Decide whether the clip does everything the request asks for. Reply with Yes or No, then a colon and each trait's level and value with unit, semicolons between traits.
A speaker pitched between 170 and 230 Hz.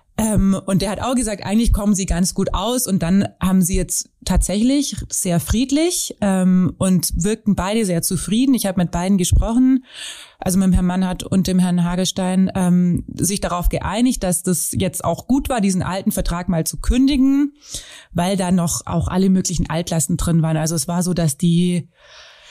Yes: medium, 185 Hz